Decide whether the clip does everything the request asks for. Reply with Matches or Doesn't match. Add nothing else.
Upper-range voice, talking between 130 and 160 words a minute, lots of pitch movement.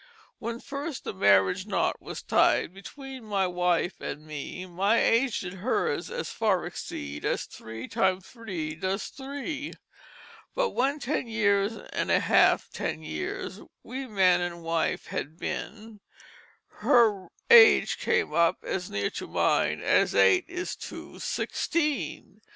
Matches